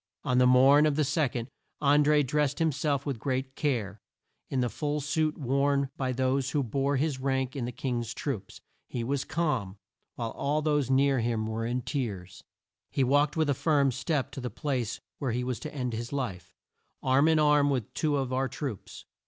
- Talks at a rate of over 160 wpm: Yes, average, 200 wpm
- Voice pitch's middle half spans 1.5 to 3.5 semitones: Yes, average, 2.7 semitones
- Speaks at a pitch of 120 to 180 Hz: Yes, low, 135 Hz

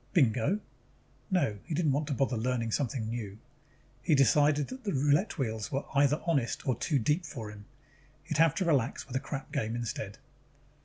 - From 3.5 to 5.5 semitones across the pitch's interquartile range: Yes, average, 4.8 semitones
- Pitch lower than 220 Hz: Yes, low, 135 Hz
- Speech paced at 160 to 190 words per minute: Yes, average, 185 wpm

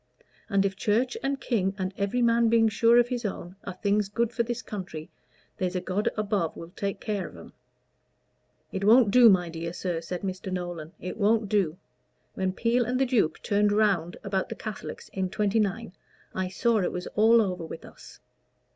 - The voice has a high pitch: Yes, high, 200 Hz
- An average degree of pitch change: Yes, average, 3.7 semitones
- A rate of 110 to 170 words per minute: No, average, 190 wpm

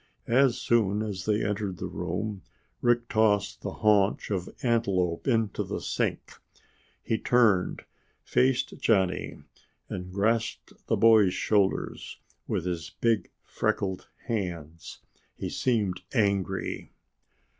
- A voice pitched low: Yes, low, 105 Hz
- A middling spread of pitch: Yes, average, 3.4 semitones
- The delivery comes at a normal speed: No, slow, 115 wpm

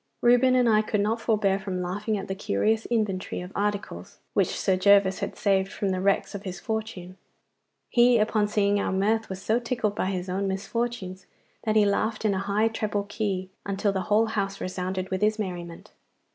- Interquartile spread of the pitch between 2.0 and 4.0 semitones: Yes, narrow, 2.4 semitones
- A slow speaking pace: No, average, 195 wpm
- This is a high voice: Yes, high, 200 Hz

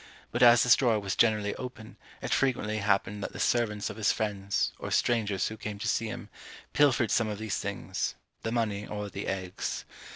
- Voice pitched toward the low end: Yes, low, 110 Hz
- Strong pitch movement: No, narrow, 2.5 semitones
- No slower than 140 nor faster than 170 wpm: No, average, 195 wpm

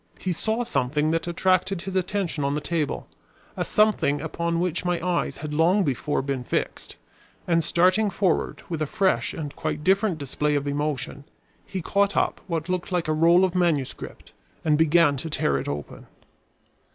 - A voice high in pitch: No, medium, 165 Hz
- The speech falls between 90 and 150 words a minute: No, average, 175 wpm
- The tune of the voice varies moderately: Yes, average, 3.7 semitones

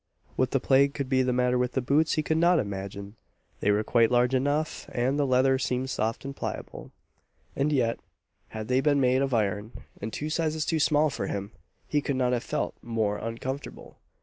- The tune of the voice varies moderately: Yes, average, 3.6 semitones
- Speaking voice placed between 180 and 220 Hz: No, low, 130 Hz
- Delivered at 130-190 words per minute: No, fast, 205 wpm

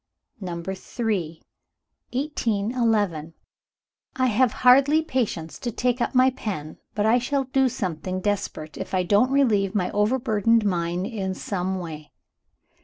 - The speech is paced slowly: Yes, slow, 130 wpm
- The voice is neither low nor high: No, high, 210 Hz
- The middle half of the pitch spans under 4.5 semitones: No, wide, 5.4 semitones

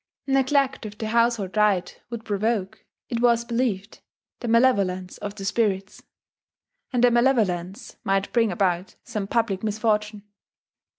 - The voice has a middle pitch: No, high, 215 Hz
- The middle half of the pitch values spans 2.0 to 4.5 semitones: Yes, average, 3.3 semitones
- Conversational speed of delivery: No, slow, 130 wpm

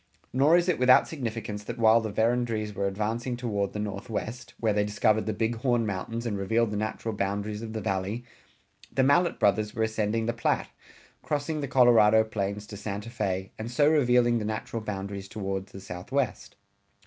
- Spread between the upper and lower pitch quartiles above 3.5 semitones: No, narrow, 2.6 semitones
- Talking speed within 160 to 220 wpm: Yes, average, 185 wpm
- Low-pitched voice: Yes, low, 110 Hz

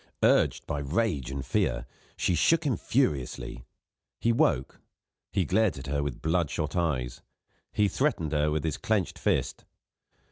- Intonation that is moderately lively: No, wide, 7.6 semitones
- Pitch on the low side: Yes, very low, 75 Hz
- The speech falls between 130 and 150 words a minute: Yes, average, 145 wpm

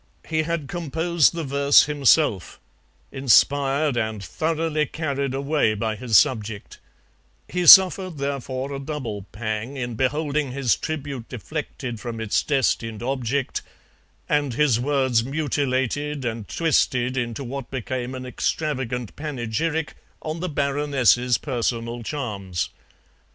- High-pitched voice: No, low, 135 Hz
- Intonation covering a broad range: No, average, 3.9 semitones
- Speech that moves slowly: Yes, slow, 120 wpm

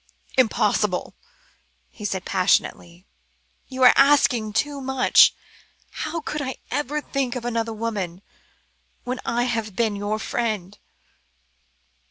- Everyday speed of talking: No, slow, 115 wpm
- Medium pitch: No, high, 230 Hz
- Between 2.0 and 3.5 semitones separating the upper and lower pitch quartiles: No, average, 4.0 semitones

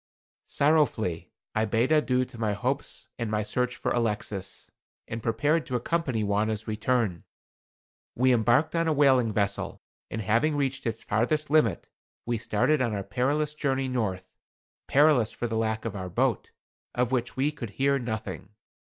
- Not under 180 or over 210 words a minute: No, average, 160 wpm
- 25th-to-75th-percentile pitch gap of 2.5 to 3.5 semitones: No, average, 4.1 semitones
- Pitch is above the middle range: No, low, 120 Hz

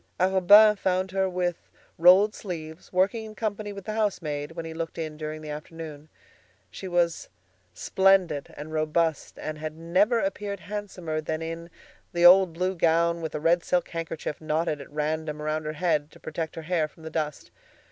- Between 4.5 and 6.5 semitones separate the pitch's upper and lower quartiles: No, average, 3.2 semitones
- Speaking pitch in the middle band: Yes, medium, 165 Hz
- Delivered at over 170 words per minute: Yes, average, 180 wpm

